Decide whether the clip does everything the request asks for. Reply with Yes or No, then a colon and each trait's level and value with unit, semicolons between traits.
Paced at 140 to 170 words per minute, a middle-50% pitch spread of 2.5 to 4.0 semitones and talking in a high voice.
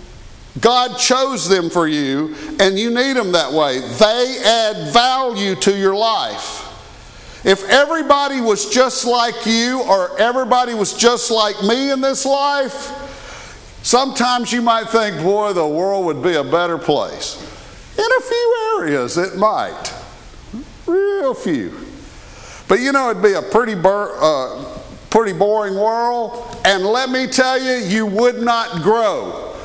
No: average, 150 wpm; average, 4.6 semitones; high, 230 Hz